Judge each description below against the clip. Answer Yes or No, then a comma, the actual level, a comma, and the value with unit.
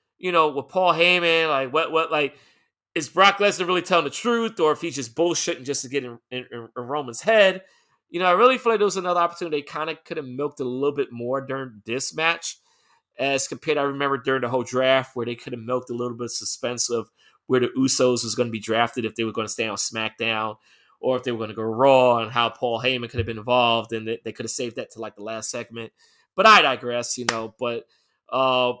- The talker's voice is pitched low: Yes, low, 130 Hz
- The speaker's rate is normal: No, fast, 255 wpm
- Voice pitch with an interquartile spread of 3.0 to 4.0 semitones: No, average, 4.7 semitones